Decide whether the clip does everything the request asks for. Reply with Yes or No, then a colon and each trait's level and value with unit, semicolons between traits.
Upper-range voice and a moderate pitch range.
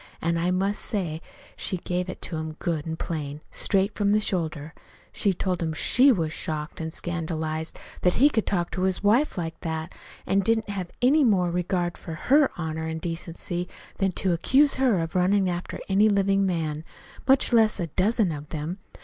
No: medium, 180 Hz; average, 3.8 semitones